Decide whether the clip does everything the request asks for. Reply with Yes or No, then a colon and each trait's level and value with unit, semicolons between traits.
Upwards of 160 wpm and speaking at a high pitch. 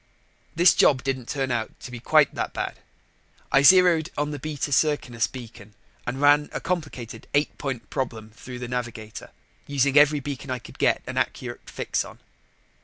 No: average, 175 wpm; low, 135 Hz